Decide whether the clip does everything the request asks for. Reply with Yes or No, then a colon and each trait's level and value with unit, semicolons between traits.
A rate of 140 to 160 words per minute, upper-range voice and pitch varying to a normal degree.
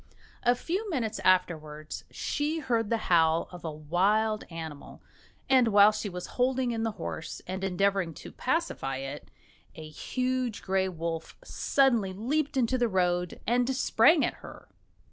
No: average, 150 wpm; high, 205 Hz; wide, 6.4 semitones